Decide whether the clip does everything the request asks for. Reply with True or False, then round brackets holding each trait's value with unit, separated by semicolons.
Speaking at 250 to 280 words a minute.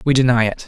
True (265 wpm)